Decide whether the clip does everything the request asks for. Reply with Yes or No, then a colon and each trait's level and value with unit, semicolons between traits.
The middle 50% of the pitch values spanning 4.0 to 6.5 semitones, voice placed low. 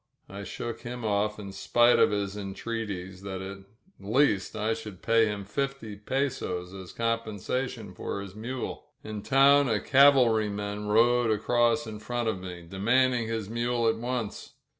No: average, 3.1 semitones; low, 110 Hz